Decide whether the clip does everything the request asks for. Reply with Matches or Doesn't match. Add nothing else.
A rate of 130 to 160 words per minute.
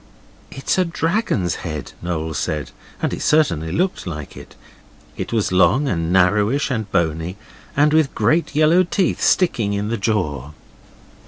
Matches